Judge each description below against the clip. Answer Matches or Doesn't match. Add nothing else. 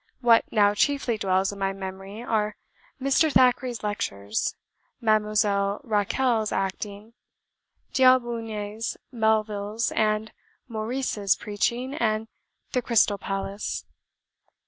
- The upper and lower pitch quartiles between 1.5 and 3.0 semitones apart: Matches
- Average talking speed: Doesn't match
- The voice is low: Doesn't match